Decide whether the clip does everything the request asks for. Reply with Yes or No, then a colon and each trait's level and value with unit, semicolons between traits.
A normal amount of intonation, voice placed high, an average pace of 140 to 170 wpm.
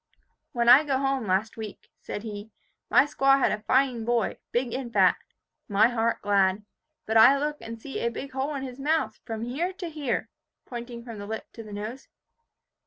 No: average, 3.6 semitones; high, 240 Hz; average, 195 wpm